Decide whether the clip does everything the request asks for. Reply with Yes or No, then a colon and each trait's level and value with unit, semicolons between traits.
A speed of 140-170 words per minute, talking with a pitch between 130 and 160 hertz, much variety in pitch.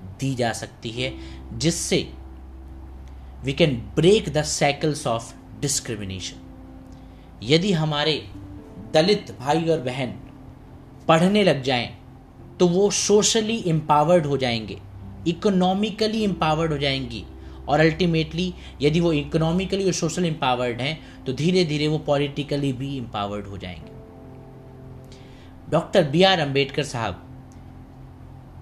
No: average, 115 wpm; low, 135 Hz; wide, 6.0 semitones